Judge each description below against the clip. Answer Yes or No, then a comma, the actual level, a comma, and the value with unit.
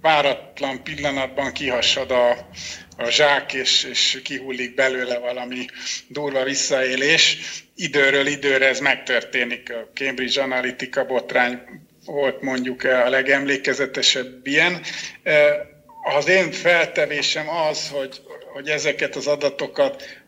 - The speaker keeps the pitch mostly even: Yes, narrow, 2.2 semitones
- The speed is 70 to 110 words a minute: Yes, slow, 105 wpm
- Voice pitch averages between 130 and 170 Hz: Yes, low, 135 Hz